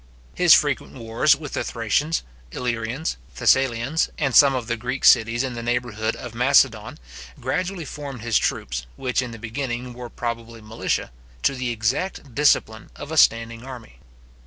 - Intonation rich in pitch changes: No, average, 2.8 semitones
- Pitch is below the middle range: Yes, low, 120 Hz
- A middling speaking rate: Yes, average, 160 wpm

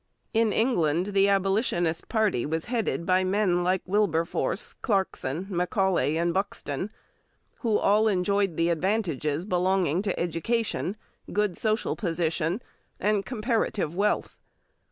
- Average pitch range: Yes, average, 3.7 semitones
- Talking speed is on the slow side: Yes, slow, 115 wpm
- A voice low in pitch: No, high, 190 Hz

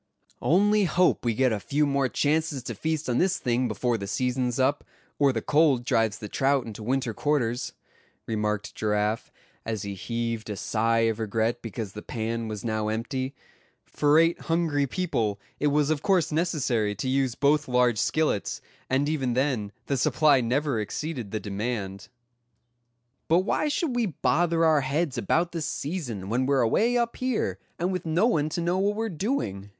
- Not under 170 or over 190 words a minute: Yes, average, 175 wpm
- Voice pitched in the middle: No, low, 130 Hz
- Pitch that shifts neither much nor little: No, wide, 5.9 semitones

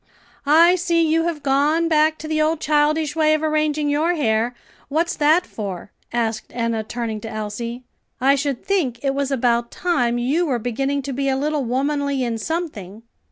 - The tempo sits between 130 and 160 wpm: No, average, 180 wpm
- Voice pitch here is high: Yes, very high, 280 Hz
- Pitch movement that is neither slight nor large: Yes, average, 4.5 semitones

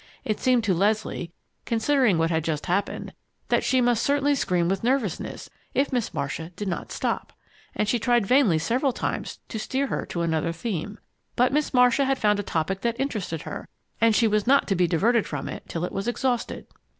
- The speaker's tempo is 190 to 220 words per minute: Yes, average, 200 wpm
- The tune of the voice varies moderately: No, wide, 6.0 semitones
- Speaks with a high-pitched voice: Yes, high, 215 Hz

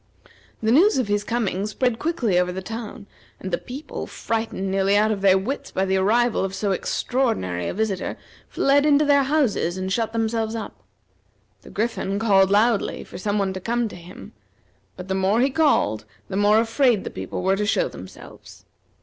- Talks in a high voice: Yes, high, 210 Hz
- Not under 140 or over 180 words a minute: No, average, 190 wpm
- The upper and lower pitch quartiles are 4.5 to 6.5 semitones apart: No, average, 3.9 semitones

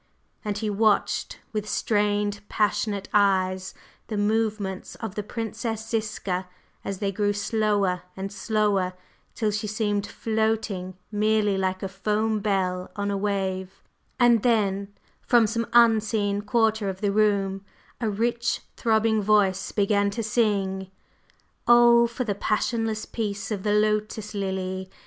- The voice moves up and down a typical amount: No, narrow, 1.9 semitones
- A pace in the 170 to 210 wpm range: No, slow, 135 wpm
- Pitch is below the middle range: No, high, 210 Hz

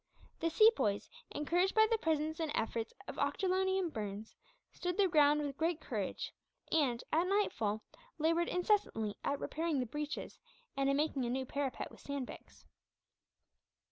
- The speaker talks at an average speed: Yes, average, 150 wpm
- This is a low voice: No, very high, 300 Hz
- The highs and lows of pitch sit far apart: No, average, 5.0 semitones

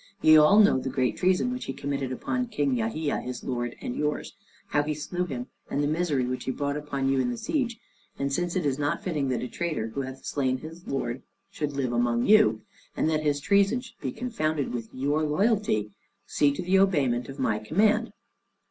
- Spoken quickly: Yes, fast, 210 wpm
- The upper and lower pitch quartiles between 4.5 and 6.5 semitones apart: Yes, wide, 5.4 semitones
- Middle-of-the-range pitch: Yes, medium, 145 Hz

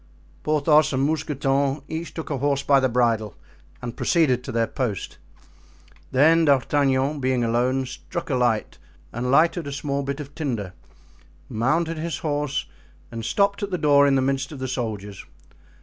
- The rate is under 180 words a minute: Yes, average, 165 wpm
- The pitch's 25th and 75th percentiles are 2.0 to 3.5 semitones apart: Yes, average, 3.2 semitones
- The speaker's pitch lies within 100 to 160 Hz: Yes, medium, 140 Hz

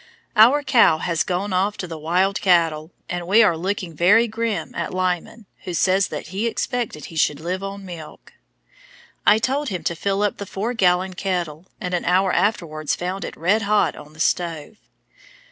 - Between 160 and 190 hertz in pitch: Yes, medium, 185 Hz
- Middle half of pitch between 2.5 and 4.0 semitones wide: Yes, average, 3.4 semitones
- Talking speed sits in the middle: Yes, average, 185 wpm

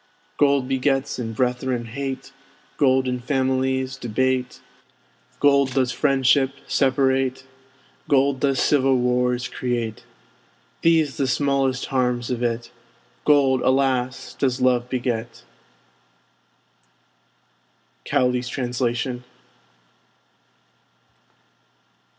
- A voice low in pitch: Yes, low, 130 Hz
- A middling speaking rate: No, slow, 85 wpm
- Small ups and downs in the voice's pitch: Yes, narrow, 1.5 semitones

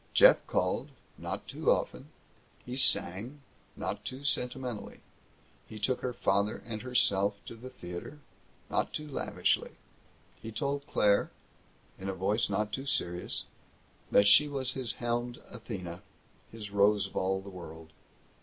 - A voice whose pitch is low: Yes, low, 110 Hz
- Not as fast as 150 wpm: Yes, average, 140 wpm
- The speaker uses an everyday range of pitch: Yes, average, 4.7 semitones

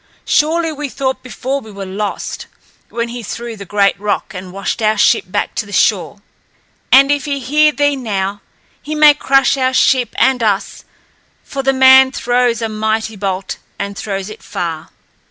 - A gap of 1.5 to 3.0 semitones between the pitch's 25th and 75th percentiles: No, average, 5.0 semitones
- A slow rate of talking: No, average, 175 wpm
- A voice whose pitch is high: Yes, high, 235 Hz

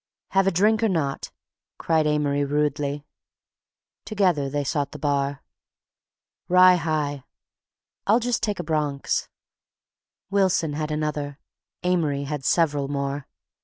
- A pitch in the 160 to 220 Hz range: No, medium, 150 Hz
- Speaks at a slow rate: Yes, slow, 120 wpm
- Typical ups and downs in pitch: Yes, average, 3.9 semitones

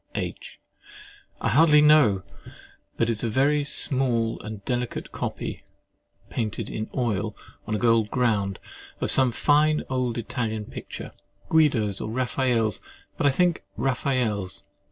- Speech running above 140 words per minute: No, slow, 135 wpm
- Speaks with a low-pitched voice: Yes, low, 120 Hz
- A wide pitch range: No, average, 4.0 semitones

